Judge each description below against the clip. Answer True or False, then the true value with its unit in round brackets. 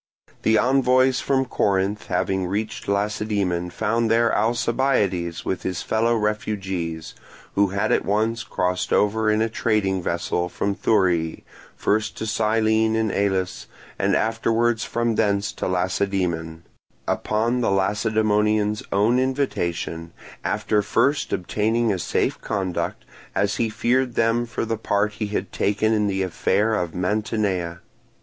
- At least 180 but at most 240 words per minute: False (135 wpm)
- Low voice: True (105 Hz)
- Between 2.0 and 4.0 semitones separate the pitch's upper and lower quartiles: True (2.9 semitones)